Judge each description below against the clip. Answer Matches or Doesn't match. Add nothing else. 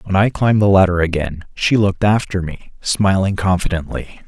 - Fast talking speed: Doesn't match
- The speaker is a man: Matches